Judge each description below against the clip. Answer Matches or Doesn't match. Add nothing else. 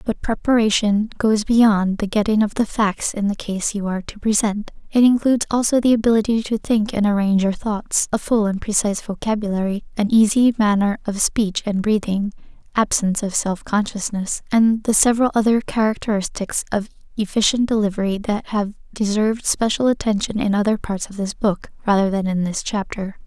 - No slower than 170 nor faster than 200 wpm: Matches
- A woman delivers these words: Matches